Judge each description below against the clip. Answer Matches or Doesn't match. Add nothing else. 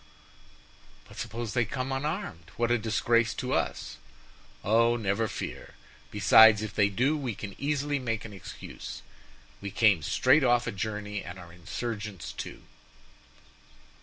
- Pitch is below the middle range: Matches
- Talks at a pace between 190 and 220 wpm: Doesn't match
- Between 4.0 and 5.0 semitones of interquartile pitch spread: Doesn't match